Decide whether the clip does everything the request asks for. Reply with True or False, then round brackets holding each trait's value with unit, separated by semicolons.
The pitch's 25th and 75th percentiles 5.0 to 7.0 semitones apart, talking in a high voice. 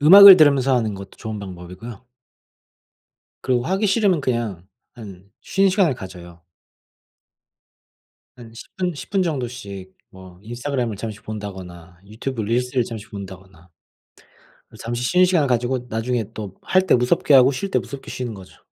False (5.6 semitones; 120 Hz)